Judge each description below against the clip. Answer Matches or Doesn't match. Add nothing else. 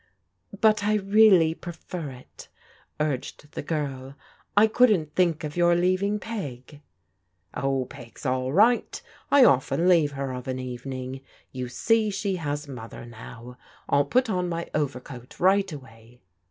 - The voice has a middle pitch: Matches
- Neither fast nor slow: Matches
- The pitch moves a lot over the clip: Matches